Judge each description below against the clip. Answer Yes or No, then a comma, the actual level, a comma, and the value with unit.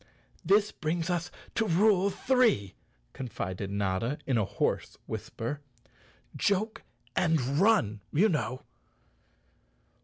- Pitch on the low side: No, medium, 160 Hz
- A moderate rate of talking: No, slow, 100 wpm